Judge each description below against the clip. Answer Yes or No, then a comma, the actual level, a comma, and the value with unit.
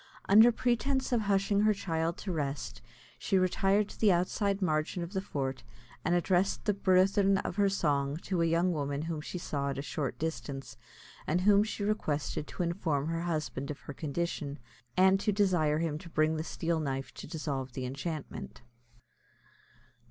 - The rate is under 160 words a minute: No, average, 175 wpm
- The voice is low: No, medium, 170 Hz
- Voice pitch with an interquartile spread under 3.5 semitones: No, average, 4.8 semitones